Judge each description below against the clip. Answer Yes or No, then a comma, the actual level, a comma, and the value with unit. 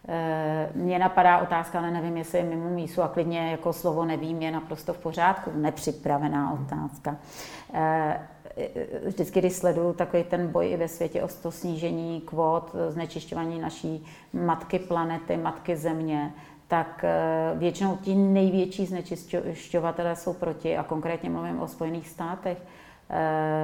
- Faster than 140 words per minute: No, average, 130 wpm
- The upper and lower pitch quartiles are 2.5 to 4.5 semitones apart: No, narrow, 1.8 semitones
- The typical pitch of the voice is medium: Yes, medium, 165 Hz